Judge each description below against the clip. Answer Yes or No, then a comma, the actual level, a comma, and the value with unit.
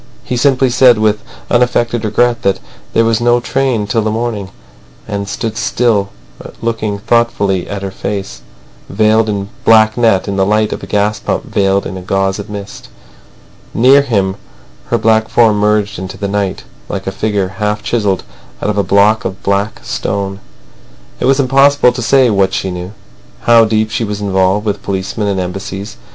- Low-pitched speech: Yes, low, 105 Hz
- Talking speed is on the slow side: No, average, 175 wpm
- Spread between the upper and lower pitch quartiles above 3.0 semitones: No, average, 2.7 semitones